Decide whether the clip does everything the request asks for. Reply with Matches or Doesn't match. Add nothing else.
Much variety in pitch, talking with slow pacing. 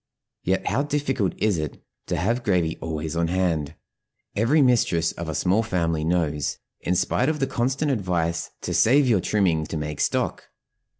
Doesn't match